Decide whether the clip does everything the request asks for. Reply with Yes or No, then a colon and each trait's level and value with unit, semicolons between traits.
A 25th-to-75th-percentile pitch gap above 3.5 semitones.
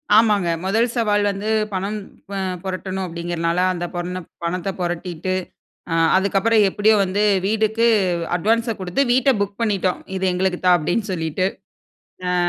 No: average, 3.1 semitones